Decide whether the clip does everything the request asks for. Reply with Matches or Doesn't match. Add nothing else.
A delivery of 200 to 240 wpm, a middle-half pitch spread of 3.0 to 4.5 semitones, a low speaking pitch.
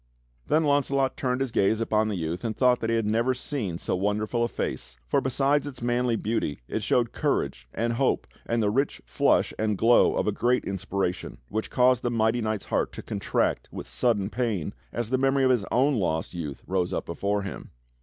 Matches